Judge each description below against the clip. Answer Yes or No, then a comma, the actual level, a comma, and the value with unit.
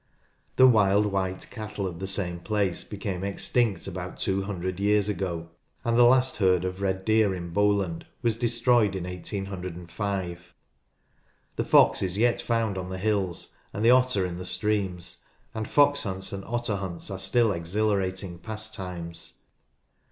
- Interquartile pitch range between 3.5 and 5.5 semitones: No, average, 2.9 semitones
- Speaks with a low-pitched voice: Yes, low, 100 Hz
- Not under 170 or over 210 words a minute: No, average, 160 wpm